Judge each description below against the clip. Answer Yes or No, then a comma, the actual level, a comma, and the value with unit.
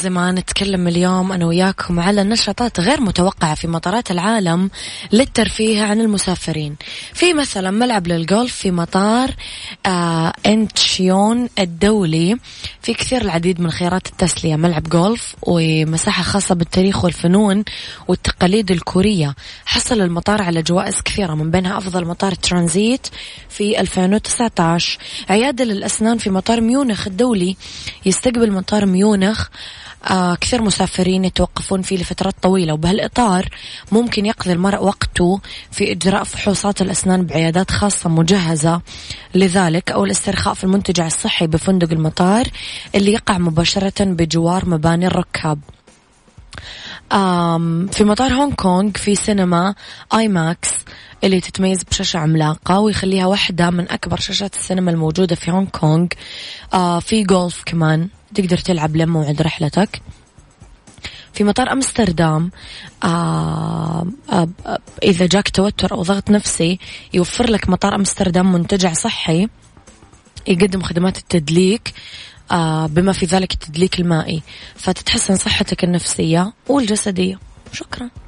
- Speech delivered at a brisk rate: No, average, 120 wpm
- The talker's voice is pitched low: No, medium, 185 Hz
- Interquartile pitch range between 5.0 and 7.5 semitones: No, average, 3.1 semitones